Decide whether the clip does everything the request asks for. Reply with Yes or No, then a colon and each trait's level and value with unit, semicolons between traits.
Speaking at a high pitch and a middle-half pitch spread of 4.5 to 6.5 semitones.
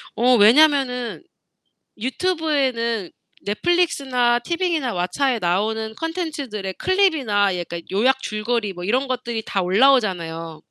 Yes: high, 240 Hz; wide, 5.5 semitones